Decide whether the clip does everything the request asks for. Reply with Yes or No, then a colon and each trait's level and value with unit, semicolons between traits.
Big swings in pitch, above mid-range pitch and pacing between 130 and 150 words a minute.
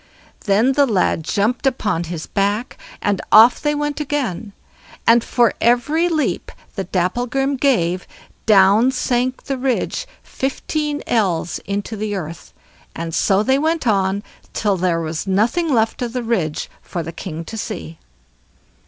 Yes: wide, 5.7 semitones; high, 220 Hz; average, 145 wpm